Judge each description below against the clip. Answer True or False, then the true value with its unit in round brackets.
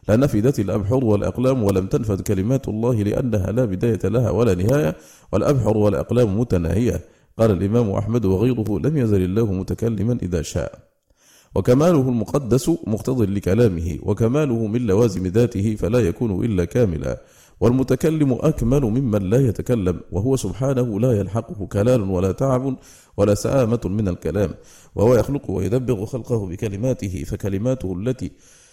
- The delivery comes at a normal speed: True (125 wpm)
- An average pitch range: True (4.5 semitones)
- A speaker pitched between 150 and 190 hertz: False (115 Hz)